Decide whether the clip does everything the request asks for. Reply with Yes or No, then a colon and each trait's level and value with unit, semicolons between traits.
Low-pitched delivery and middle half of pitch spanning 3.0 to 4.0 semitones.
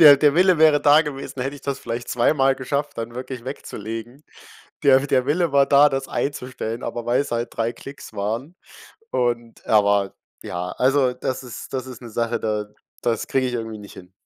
Yes: low, 130 Hz; average, 3.4 semitones